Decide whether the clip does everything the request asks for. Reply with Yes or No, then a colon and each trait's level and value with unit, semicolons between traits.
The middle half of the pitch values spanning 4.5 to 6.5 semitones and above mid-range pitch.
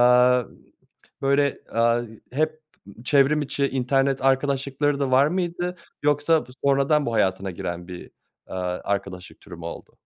No: average, 4.9 semitones; low, 135 Hz